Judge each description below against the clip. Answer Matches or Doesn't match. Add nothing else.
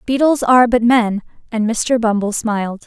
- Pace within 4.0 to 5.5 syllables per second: Matches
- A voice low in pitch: Doesn't match